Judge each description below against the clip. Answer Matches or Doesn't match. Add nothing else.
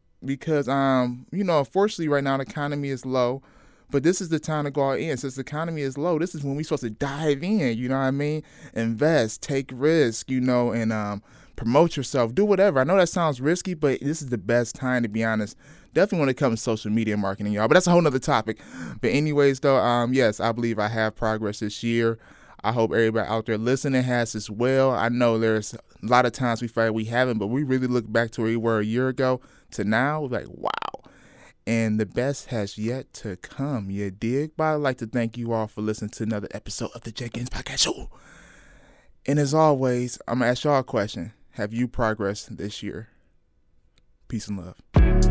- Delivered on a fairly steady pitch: Doesn't match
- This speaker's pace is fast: Matches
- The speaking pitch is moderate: Doesn't match